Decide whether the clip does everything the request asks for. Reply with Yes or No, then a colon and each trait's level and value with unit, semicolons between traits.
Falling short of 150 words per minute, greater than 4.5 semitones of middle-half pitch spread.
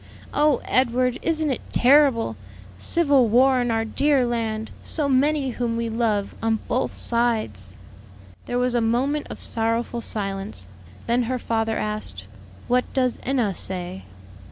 No: average, 140 wpm; average, 2.7 semitones